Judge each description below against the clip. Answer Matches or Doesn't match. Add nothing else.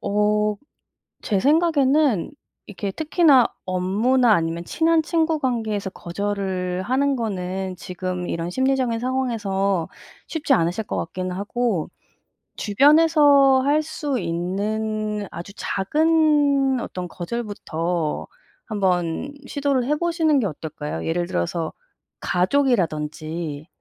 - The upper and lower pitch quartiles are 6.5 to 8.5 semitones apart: Matches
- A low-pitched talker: Doesn't match